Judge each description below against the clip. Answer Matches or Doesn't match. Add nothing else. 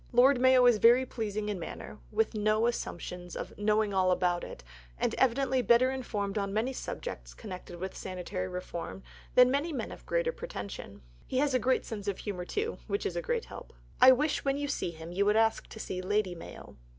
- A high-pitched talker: Matches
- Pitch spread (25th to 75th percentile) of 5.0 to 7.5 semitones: Matches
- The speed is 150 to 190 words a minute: Doesn't match